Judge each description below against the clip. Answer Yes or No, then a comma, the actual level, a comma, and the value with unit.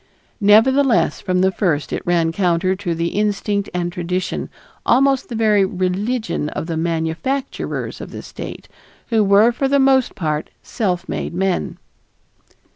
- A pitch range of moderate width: Yes, average, 4.5 semitones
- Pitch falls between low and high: No, high, 195 Hz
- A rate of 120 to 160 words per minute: Yes, average, 150 wpm